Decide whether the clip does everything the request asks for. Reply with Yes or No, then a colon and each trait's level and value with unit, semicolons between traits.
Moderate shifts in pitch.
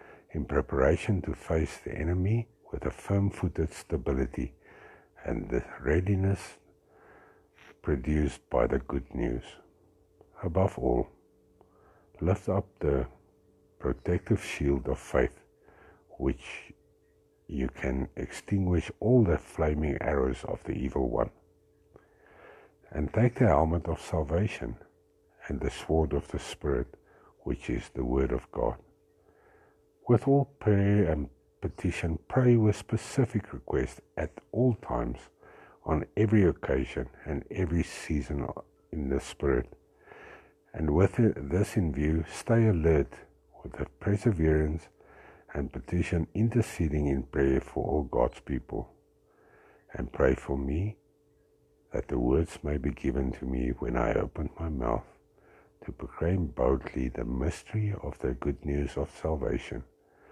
No: wide, 5.9 semitones